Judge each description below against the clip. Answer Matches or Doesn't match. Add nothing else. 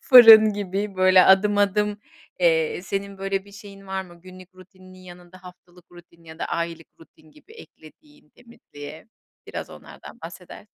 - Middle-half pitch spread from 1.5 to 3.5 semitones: Matches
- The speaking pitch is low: Doesn't match